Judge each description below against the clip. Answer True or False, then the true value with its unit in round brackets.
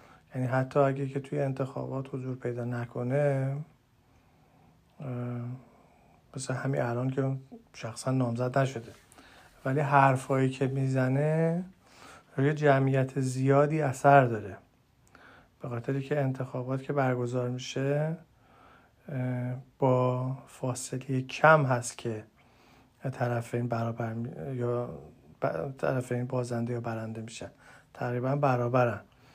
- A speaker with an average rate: False (100 wpm)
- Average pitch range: False (2.1 semitones)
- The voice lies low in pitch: True (130 Hz)